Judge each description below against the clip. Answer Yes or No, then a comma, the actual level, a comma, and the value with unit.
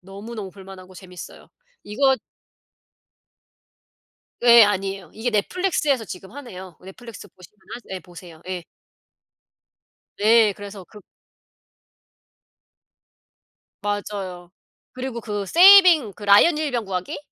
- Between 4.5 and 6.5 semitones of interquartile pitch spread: No, average, 4.0 semitones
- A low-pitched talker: No, high, 205 Hz